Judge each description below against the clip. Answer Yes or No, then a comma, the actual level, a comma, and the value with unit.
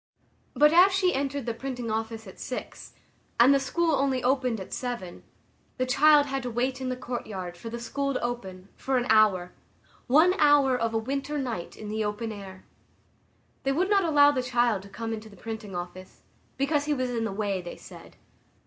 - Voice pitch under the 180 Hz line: No, high, 245 Hz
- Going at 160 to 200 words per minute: Yes, average, 195 wpm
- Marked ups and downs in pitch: No, average, 4.2 semitones